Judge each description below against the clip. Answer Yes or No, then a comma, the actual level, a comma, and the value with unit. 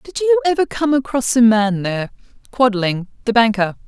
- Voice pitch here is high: Yes, high, 225 Hz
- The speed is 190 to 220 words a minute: No, average, 170 wpm